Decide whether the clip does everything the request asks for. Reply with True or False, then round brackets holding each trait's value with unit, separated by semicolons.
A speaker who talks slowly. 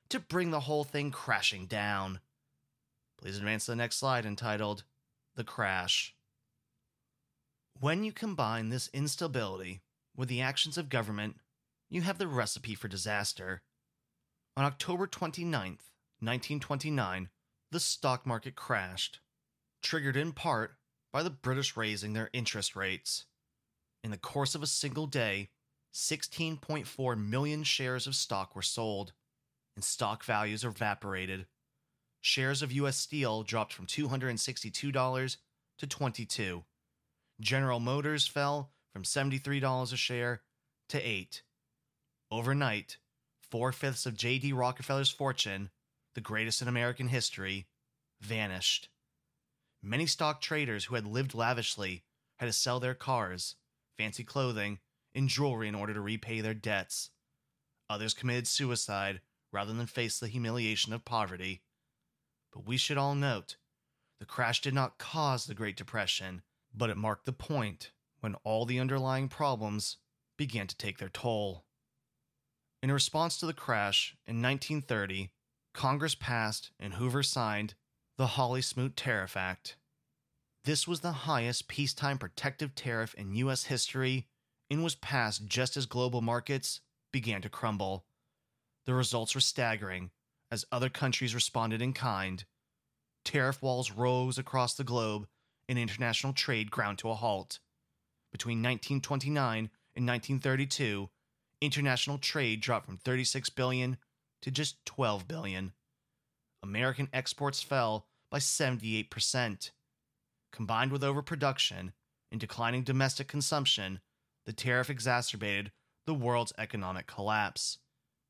True (125 wpm)